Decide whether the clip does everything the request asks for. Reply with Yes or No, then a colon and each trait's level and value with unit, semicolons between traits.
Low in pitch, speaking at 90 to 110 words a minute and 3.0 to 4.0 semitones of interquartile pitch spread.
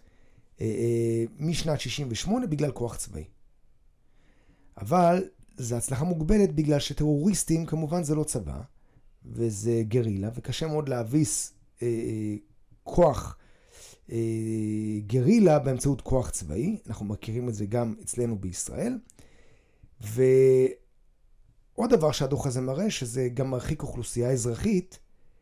No: low, 130 Hz; average, 105 wpm; average, 5.0 semitones